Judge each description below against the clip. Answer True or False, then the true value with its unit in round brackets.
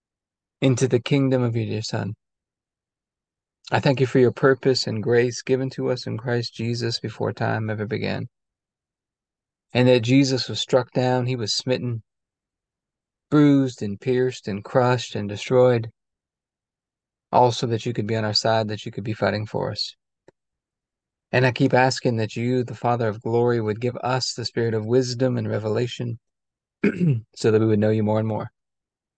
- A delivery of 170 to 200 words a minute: True (175 wpm)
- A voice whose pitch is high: False (120 Hz)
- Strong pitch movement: False (2.7 semitones)